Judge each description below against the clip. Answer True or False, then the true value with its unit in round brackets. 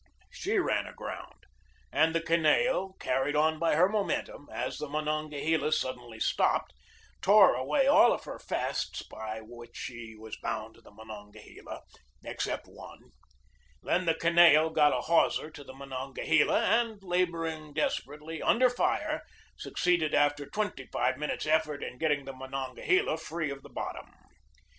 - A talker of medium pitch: True (155 Hz)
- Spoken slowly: False (150 wpm)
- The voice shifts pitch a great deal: False (4.2 semitones)